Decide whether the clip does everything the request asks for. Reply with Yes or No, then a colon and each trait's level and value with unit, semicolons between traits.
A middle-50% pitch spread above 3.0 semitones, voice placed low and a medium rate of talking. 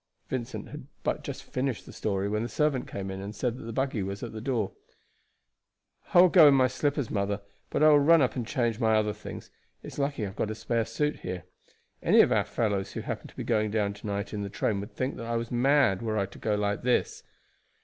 No: average, 4.2 semitones; low, 115 Hz; fast, 250 wpm